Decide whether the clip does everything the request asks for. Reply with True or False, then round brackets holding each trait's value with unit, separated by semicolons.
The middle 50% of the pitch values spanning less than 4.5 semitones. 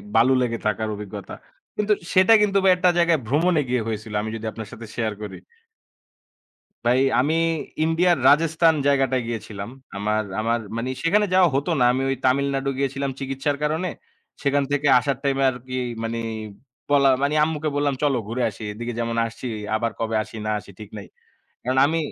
False (4.8 semitones)